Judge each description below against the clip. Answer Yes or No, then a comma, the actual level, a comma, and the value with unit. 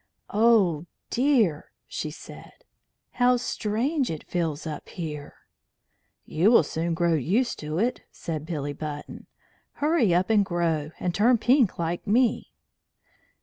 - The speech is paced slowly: Yes, slow, 130 wpm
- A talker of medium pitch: Yes, medium, 180 Hz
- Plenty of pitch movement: Yes, wide, 6.8 semitones